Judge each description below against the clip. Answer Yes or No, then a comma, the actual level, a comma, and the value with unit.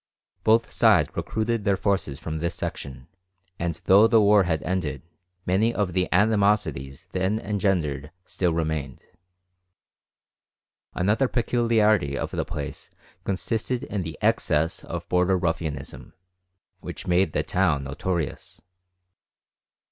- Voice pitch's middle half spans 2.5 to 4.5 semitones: No, average, 4.9 semitones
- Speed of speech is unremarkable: No, slow, 120 wpm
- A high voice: No, very low, 90 Hz